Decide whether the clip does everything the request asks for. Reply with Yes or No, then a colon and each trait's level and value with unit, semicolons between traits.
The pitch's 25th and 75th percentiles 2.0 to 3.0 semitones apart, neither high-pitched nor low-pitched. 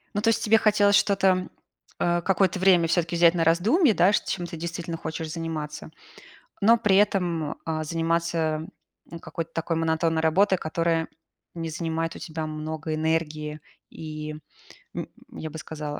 Yes: narrow, 2.5 semitones; medium, 165 Hz